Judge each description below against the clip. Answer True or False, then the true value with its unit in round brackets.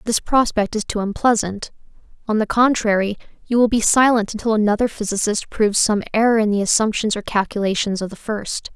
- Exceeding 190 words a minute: False (180 wpm)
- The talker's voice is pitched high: True (215 Hz)